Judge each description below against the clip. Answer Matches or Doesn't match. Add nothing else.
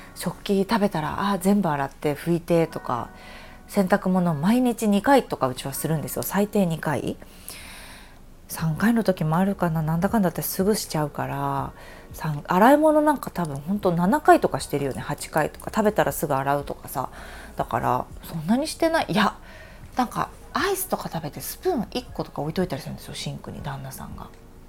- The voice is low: Doesn't match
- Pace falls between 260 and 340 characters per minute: Doesn't match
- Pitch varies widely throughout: Matches